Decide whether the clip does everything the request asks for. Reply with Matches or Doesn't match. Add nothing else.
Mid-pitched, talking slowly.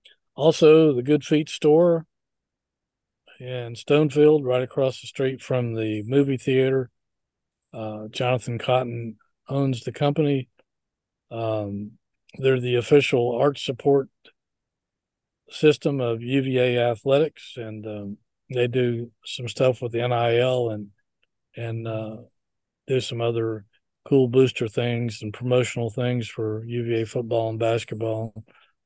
Doesn't match